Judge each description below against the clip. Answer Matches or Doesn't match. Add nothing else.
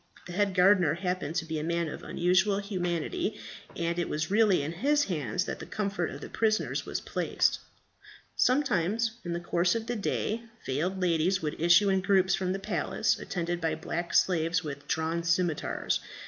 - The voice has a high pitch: Doesn't match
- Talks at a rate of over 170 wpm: Matches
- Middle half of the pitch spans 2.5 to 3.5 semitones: Matches